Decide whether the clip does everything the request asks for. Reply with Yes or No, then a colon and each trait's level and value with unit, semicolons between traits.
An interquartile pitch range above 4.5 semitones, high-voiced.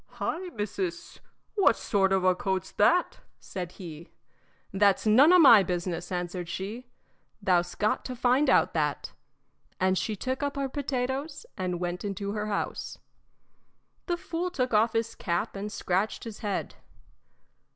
Yes: wide, 5.5 semitones; high, 205 Hz